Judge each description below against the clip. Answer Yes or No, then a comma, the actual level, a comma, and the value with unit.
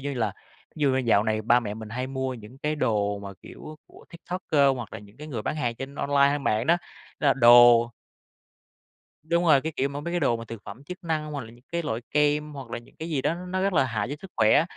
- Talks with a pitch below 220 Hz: Yes, low, 135 Hz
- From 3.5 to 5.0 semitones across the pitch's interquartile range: Yes, average, 4.7 semitones